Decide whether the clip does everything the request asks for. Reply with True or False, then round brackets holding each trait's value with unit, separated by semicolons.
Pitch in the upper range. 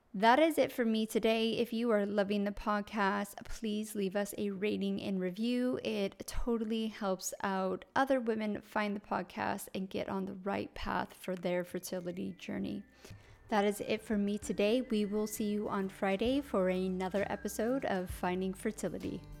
True (205 Hz)